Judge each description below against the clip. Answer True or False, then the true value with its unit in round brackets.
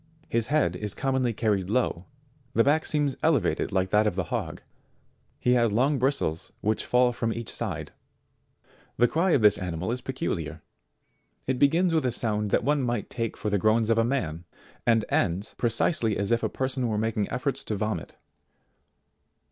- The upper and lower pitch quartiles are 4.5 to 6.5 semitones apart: False (3.9 semitones)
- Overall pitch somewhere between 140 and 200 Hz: False (115 Hz)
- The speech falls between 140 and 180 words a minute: False (190 wpm)